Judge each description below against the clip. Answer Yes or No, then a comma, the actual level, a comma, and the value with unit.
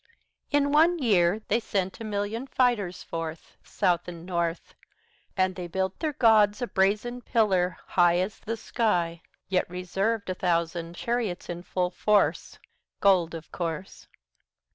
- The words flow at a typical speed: Yes, average, 145 wpm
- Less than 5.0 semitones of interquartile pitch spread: Yes, average, 4.2 semitones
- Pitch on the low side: No, high, 190 Hz